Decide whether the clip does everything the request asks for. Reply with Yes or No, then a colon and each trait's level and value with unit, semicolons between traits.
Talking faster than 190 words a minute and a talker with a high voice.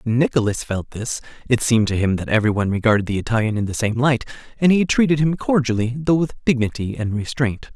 No: average, 200 wpm; low, 120 Hz